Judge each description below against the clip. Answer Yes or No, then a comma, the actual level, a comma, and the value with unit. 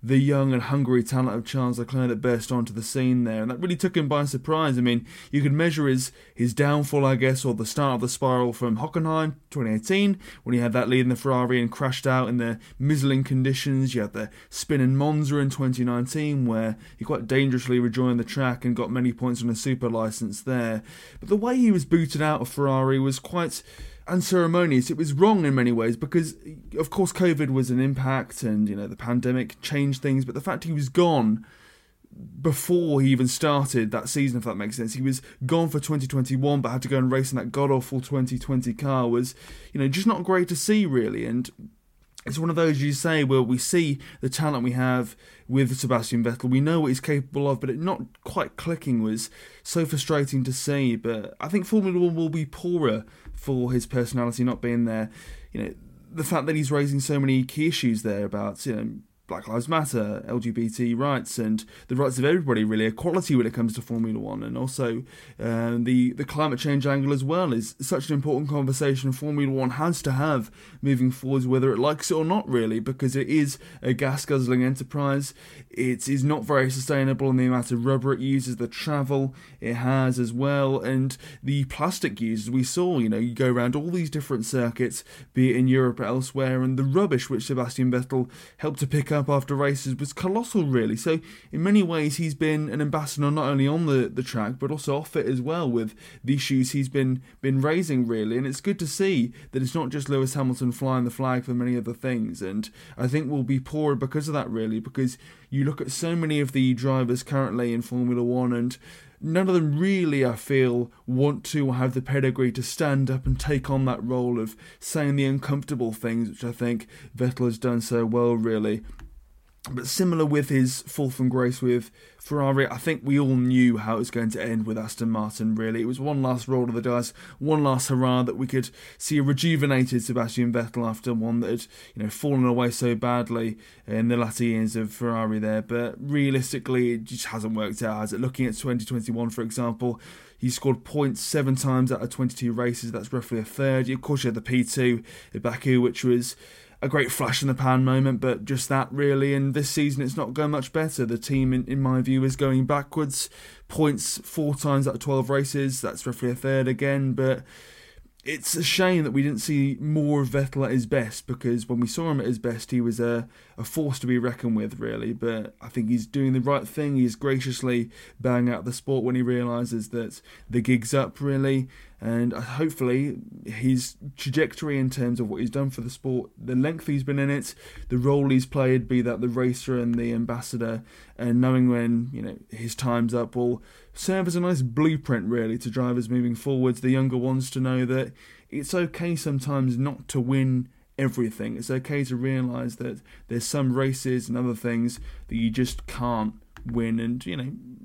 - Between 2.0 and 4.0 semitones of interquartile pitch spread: Yes, average, 2.8 semitones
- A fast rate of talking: Yes, fast, 210 wpm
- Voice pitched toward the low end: Yes, low, 130 Hz